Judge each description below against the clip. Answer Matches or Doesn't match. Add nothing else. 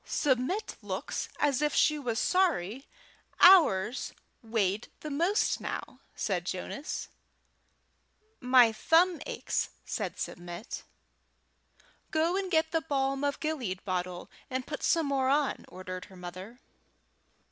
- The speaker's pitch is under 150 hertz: Doesn't match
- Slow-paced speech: Matches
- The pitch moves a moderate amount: Doesn't match